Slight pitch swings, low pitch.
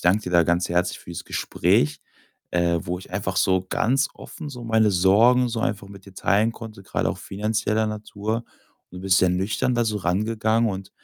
No: average, 3.5 semitones; low, 100 Hz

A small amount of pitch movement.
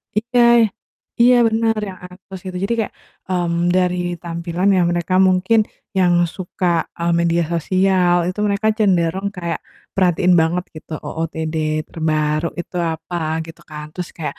Yes: narrow, 2.3 semitones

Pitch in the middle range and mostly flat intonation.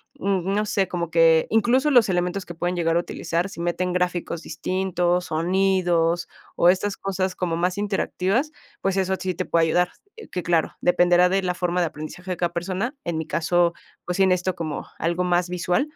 Yes: medium, 180 Hz; narrow, 1.8 semitones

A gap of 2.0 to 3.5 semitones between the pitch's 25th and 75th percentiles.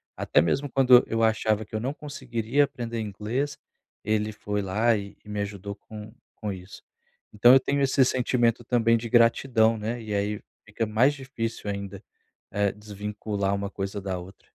Yes: average, 2.9 semitones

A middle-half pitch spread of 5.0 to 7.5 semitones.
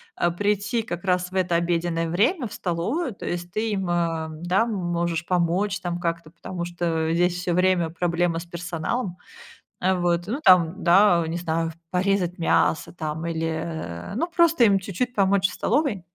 No: average, 2.7 semitones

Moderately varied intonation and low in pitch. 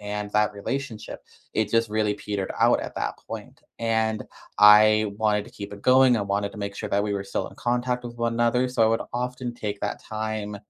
No: narrow, 2.3 semitones; low, 110 Hz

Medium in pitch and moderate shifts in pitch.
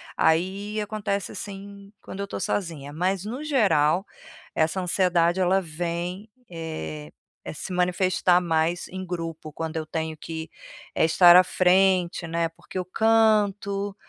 Yes: medium, 180 Hz; average, 3.1 semitones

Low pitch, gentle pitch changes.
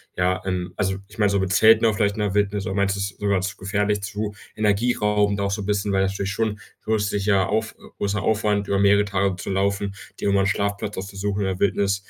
Yes: low, 100 Hz; narrow, 1.1 semitones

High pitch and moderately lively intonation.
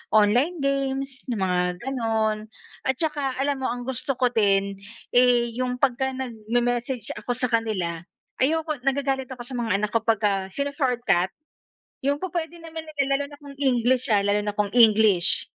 Yes: high, 245 Hz; average, 4.1 semitones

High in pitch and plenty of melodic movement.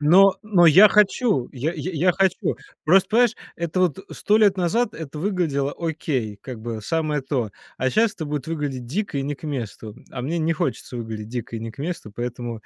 No: medium, 150 Hz; wide, 6.7 semitones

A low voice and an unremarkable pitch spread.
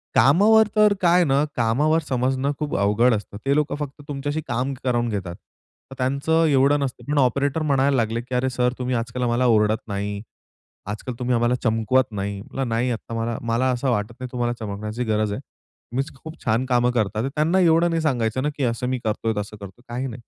Yes: low, 125 Hz; average, 3.6 semitones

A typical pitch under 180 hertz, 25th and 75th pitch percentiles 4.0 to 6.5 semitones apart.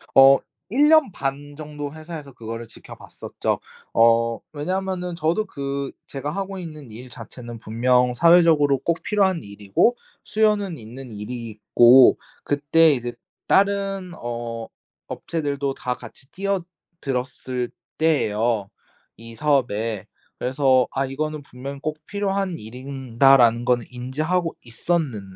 Yes: medium, 140 Hz; wide, 5.6 semitones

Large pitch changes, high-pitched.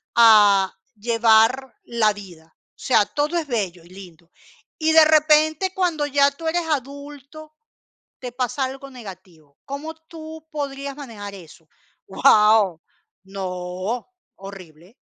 Yes: wide, 7.3 semitones; high, 240 Hz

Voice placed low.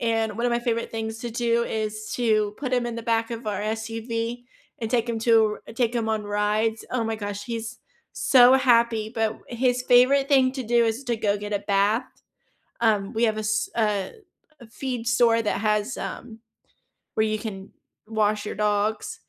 No: high, 225 Hz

